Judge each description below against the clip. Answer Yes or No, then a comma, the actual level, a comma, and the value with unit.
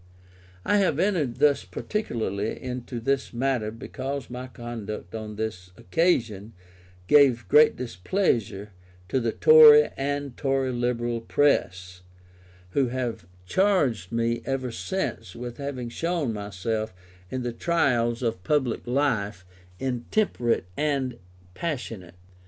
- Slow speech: Yes, slow, 115 wpm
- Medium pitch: No, low, 120 Hz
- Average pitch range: Yes, average, 4.2 semitones